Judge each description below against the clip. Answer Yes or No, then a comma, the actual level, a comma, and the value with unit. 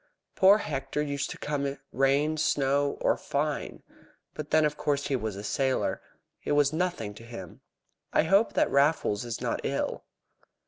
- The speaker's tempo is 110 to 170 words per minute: Yes, average, 165 wpm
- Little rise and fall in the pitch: Yes, narrow, 2.2 semitones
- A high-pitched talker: No, medium, 140 Hz